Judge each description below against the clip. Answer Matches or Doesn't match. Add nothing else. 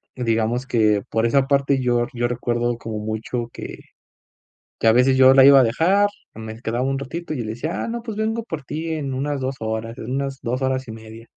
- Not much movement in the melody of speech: Doesn't match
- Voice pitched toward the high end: Doesn't match